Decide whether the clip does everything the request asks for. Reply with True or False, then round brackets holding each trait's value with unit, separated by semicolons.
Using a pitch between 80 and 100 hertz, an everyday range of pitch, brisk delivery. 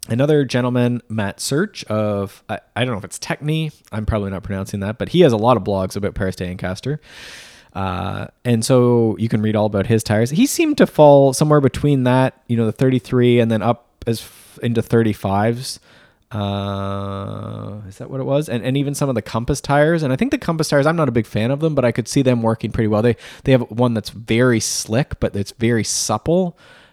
False (115 Hz; 4.5 semitones; 225 wpm)